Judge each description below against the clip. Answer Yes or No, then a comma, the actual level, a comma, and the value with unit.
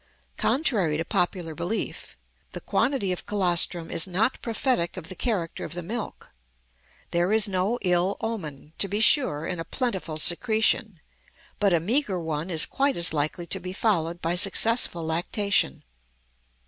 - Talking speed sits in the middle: Yes, average, 155 wpm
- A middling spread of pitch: Yes, average, 4.6 semitones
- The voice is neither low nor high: Yes, medium, 180 Hz